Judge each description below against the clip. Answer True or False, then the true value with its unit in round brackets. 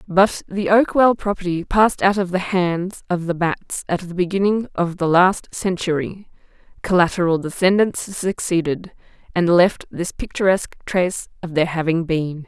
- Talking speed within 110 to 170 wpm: True (150 wpm)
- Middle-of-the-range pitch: True (180 Hz)